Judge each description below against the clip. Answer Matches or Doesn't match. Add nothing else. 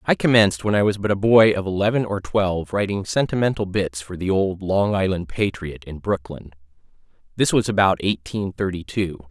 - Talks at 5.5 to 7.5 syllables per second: Doesn't match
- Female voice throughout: Doesn't match